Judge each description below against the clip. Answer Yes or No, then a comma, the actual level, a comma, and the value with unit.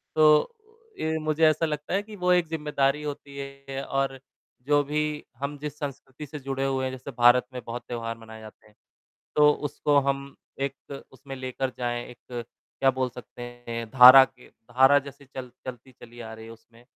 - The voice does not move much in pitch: No, average, 3.1 semitones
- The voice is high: No, low, 135 Hz